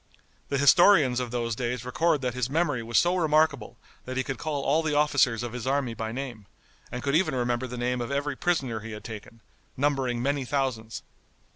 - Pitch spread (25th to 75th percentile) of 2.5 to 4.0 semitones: Yes, average, 3.1 semitones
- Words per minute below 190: No, average, 200 wpm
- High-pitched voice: No, low, 130 Hz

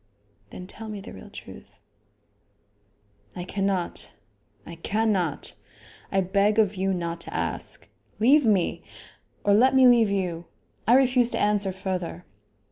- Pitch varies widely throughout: No, average, 3.5 semitones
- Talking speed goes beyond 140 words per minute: No, slow, 135 wpm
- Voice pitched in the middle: No, high, 200 Hz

